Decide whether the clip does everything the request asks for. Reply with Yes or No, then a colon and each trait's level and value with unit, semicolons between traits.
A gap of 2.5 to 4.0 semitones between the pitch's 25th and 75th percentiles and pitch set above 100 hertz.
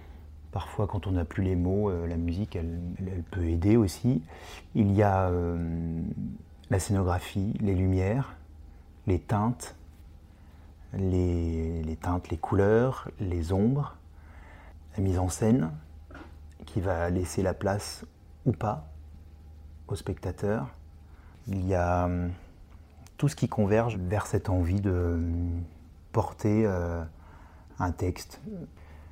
No: average, 3.4 semitones; very low, 85 Hz